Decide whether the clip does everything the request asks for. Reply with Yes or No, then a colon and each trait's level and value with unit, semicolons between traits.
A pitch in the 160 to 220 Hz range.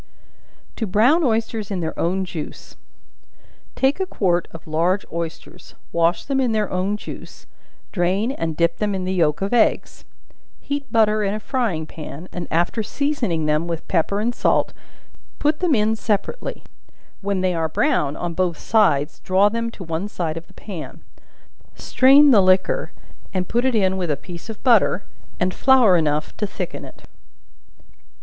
Yes: high, 190 Hz